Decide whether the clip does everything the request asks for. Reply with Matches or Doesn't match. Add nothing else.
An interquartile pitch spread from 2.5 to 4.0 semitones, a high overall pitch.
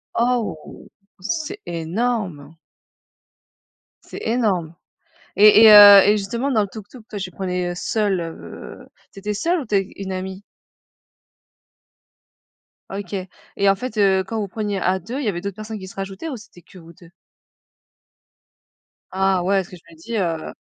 Matches